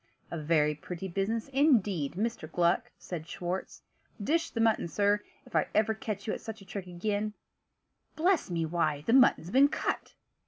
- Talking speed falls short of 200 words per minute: Yes, average, 170 wpm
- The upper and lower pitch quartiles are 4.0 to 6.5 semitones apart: Yes, average, 4.8 semitones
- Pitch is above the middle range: Yes, high, 200 Hz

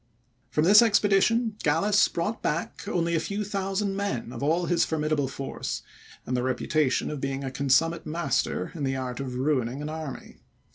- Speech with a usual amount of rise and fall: No, wide, 6.3 semitones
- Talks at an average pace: Yes, average, 175 wpm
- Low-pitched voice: No, medium, 155 Hz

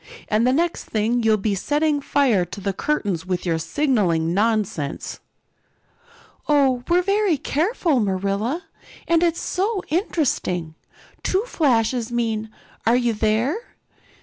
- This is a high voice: Yes, high, 240 Hz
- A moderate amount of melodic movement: No, wide, 7.1 semitones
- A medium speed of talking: No, slow, 125 wpm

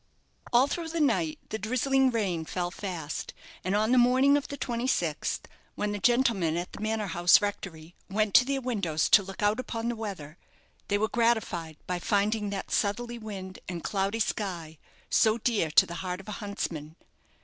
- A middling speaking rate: Yes, average, 180 wpm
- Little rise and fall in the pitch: No, average, 4.8 semitones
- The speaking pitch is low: No, high, 205 Hz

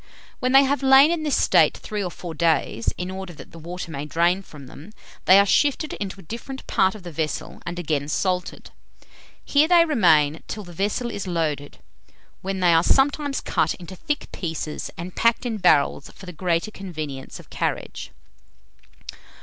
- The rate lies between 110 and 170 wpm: No, average, 180 wpm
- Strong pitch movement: Yes, wide, 6.0 semitones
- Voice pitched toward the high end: No, medium, 180 Hz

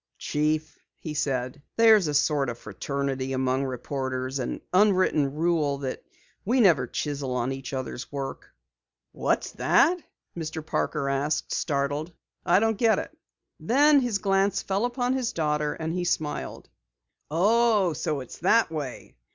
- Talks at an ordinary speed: Yes, average, 145 wpm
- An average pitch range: No, wide, 6.2 semitones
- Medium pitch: Yes, medium, 150 Hz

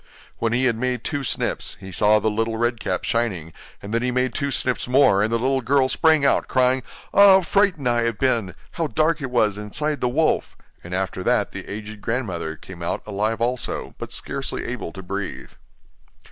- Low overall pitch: Yes, low, 120 Hz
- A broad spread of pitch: No, average, 4.1 semitones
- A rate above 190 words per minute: Yes, average, 200 wpm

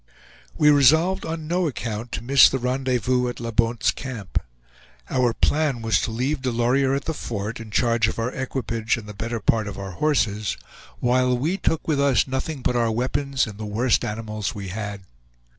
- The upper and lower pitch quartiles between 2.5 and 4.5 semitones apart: Yes, average, 3.5 semitones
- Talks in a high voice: No, low, 120 Hz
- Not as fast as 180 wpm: No, average, 190 wpm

